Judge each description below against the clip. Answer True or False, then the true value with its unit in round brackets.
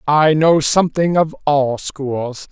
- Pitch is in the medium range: True (150 Hz)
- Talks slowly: False (145 wpm)